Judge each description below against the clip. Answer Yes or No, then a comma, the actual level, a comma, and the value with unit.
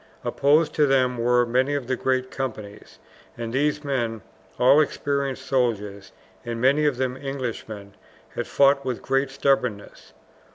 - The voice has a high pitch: No, low, 130 Hz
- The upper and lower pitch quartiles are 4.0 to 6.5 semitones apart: No, average, 2.8 semitones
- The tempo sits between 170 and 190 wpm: No, average, 140 wpm